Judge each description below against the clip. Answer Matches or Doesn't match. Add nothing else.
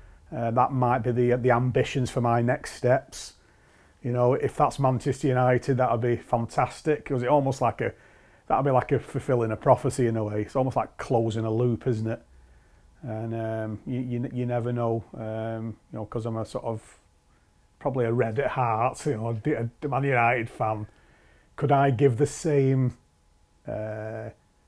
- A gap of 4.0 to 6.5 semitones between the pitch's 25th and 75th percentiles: Doesn't match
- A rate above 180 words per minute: Matches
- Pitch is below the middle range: Matches